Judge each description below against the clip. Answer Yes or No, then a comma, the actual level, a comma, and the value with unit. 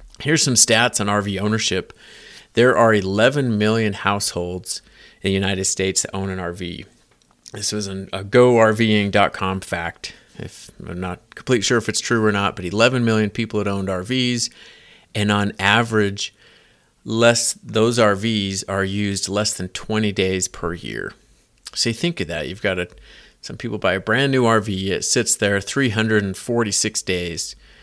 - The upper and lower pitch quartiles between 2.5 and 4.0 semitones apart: Yes, average, 2.9 semitones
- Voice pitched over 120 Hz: No, low, 105 Hz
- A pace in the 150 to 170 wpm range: Yes, average, 165 wpm